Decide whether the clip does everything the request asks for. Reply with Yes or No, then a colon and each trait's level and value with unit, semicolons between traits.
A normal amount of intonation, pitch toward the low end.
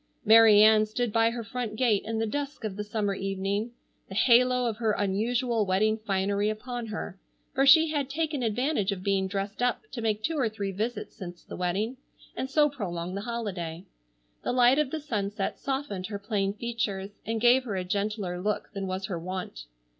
No: average, 3.7 semitones; high, 215 Hz